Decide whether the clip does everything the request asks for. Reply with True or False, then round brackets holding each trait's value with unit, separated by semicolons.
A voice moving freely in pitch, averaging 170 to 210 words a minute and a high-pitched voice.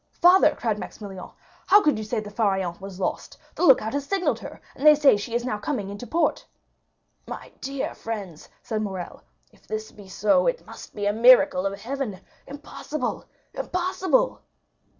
True (6.2 semitones; 175 wpm; 225 Hz)